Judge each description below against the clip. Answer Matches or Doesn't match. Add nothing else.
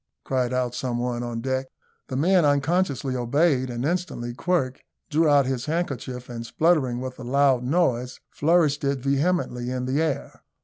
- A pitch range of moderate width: Matches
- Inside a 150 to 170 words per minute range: Matches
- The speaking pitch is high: Doesn't match